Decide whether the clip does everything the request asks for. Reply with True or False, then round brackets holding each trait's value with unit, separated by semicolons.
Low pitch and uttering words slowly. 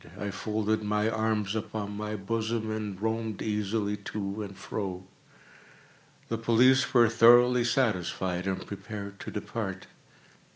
True (105 Hz; 125 wpm)